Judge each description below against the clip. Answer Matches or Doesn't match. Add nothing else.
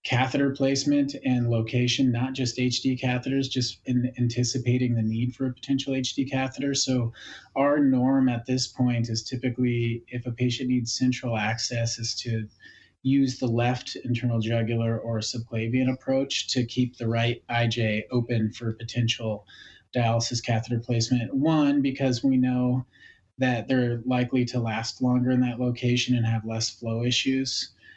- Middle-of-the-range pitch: Doesn't match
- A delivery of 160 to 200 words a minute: Doesn't match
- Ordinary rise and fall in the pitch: Doesn't match